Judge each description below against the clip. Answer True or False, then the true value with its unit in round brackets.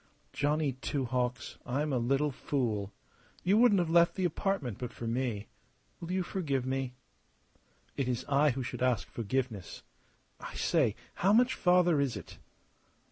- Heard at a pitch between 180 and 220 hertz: False (135 Hz)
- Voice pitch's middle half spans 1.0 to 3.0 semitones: False (5.5 semitones)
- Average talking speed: True (155 wpm)